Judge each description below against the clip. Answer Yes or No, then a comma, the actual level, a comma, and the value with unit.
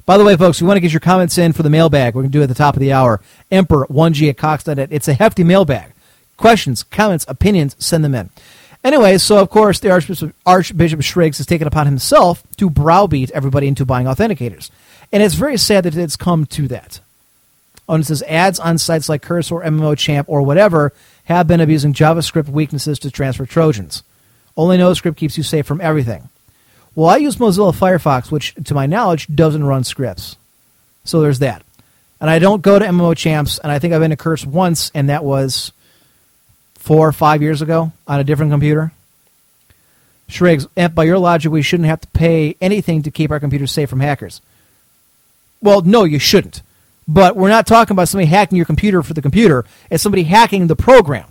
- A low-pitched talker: No, medium, 155 Hz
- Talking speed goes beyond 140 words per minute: Yes, average, 200 wpm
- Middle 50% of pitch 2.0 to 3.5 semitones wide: No, average, 4.1 semitones